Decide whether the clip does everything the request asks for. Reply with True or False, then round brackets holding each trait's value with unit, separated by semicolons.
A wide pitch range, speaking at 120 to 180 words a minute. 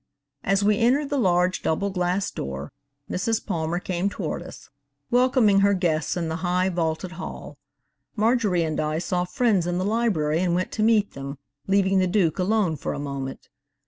False (3.8 semitones; 175 wpm)